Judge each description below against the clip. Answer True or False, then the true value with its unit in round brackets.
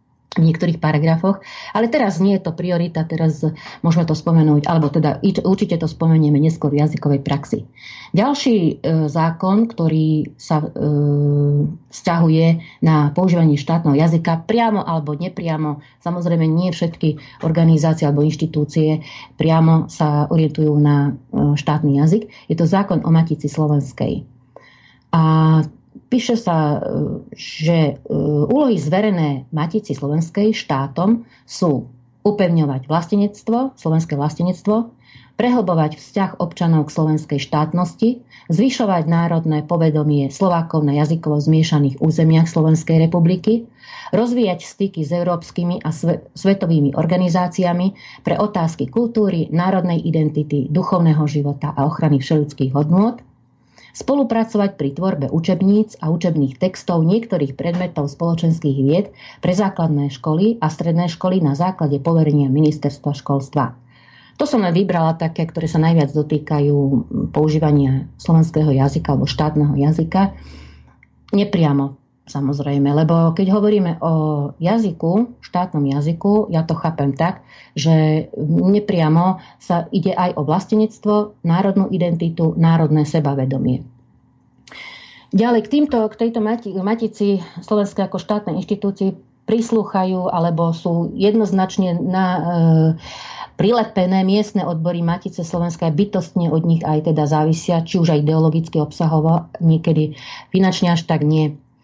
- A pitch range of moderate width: True (3.7 semitones)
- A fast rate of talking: False (115 wpm)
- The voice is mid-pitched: True (165 Hz)